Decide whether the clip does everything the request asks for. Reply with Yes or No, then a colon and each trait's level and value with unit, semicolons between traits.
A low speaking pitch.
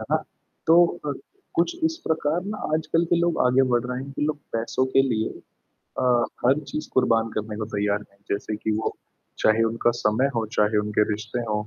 Yes: low, 115 Hz